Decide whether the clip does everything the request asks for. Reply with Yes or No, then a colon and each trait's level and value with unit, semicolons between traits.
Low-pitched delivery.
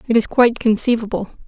No: high, 225 Hz